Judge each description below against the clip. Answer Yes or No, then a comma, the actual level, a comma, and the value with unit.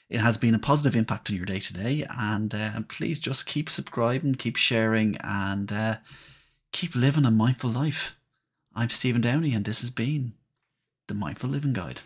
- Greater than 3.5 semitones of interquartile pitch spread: Yes, average, 4.0 semitones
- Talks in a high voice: No, low, 120 Hz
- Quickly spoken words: No, average, 185 wpm